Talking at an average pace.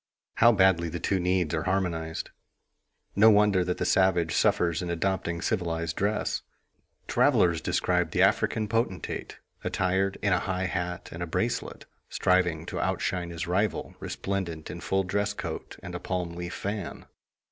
Yes: average, 155 wpm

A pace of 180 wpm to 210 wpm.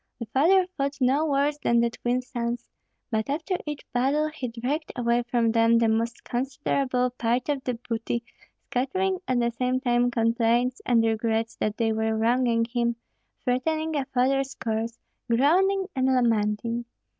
No: average, 155 wpm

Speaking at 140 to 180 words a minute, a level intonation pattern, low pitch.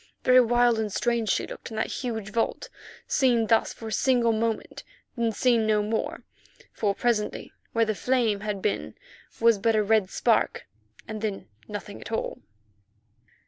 No: average, 165 wpm; narrow, 1.8 semitones; high, 225 Hz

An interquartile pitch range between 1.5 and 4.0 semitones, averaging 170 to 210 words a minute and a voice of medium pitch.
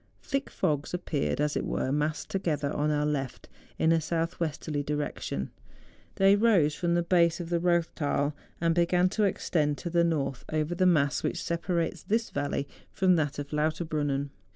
Yes: average, 2.9 semitones; average, 175 wpm; medium, 160 Hz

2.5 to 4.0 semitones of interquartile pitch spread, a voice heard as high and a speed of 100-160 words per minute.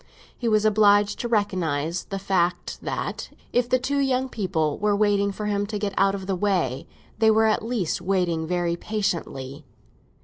No: average, 3.5 semitones; high, 200 Hz; average, 175 wpm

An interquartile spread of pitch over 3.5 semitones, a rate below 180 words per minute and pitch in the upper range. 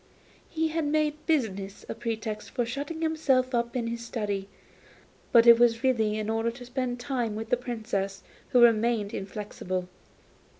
No: average, 3.0 semitones; average, 160 wpm; high, 235 Hz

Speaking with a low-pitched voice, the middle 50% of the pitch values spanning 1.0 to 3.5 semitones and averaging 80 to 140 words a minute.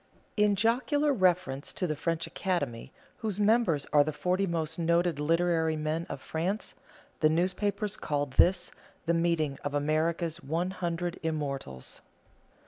No: medium, 170 Hz; average, 3.2 semitones; slow, 135 wpm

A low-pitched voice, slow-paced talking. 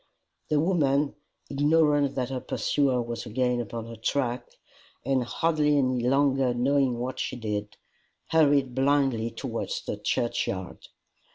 Yes: low, 130 Hz; slow, 125 wpm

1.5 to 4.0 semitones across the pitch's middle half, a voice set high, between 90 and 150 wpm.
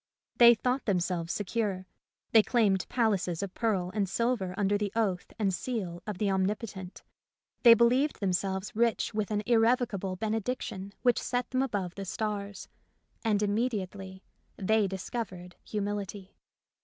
Yes: average, 3.2 semitones; high, 205 Hz; average, 145 wpm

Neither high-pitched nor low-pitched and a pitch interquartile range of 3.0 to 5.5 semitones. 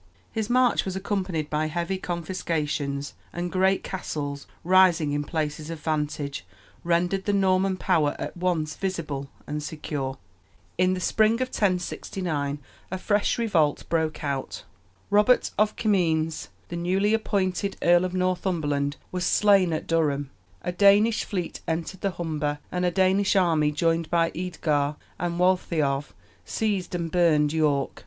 Yes: medium, 175 Hz; average, 3.7 semitones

